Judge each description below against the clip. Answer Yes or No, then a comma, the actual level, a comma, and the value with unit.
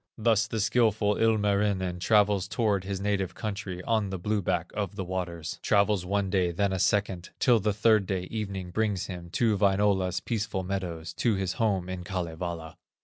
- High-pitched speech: No, low, 100 Hz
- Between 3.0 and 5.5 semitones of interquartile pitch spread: No, narrow, 2.5 semitones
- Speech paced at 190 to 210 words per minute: No, average, 175 wpm